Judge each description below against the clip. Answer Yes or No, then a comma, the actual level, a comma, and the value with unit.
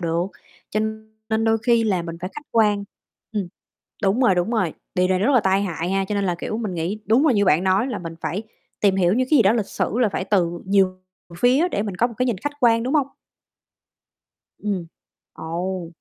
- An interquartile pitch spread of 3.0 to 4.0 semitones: Yes, average, 3.7 semitones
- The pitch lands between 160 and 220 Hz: Yes, high, 200 Hz